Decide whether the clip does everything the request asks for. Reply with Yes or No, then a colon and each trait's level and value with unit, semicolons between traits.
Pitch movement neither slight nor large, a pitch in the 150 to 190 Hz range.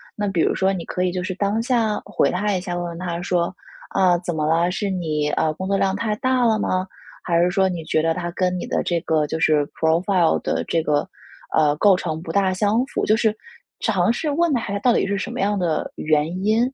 Yes: average, 3.4 semitones; medium, 185 Hz